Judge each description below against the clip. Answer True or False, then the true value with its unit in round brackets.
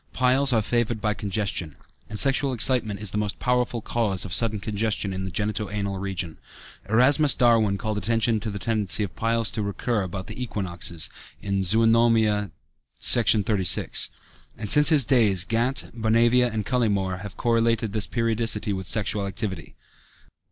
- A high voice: False (110 Hz)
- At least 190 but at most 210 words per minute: False (155 wpm)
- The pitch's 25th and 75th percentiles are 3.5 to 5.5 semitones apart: False (2.8 semitones)